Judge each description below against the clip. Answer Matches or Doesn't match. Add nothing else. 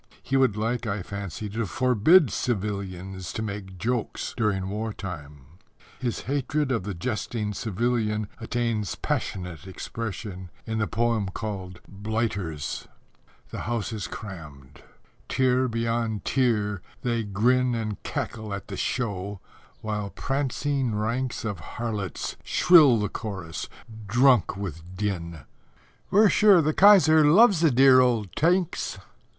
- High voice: Doesn't match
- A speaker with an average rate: Doesn't match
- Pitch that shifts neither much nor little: Matches